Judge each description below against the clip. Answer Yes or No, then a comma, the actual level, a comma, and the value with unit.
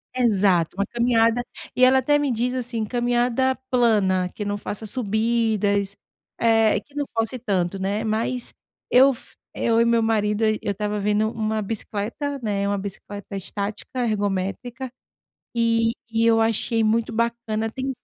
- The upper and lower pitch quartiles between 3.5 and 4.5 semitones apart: No, narrow, 2.6 semitones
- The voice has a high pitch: Yes, high, 225 Hz